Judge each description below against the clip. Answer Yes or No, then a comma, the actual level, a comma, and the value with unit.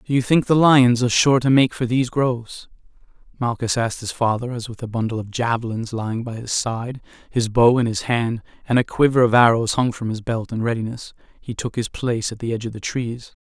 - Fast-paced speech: Yes, fast, 230 wpm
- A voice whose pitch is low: Yes, low, 120 Hz